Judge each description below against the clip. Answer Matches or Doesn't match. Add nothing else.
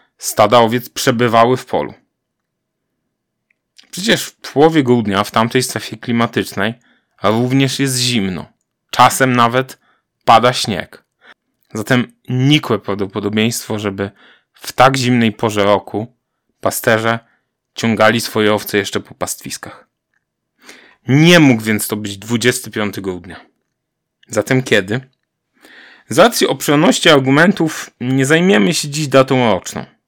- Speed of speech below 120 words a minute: Matches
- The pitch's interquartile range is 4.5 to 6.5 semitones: Doesn't match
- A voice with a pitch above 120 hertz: Doesn't match